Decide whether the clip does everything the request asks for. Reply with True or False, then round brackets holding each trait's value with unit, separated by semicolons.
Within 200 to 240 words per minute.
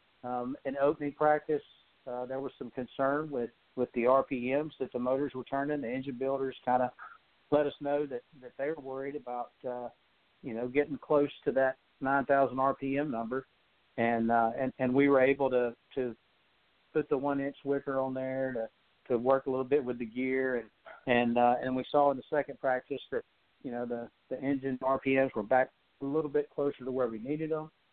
True (205 wpm)